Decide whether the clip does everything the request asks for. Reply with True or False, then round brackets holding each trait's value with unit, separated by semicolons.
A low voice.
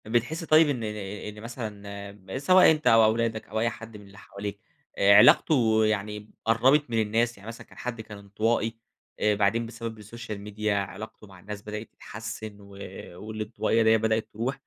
True (110 Hz)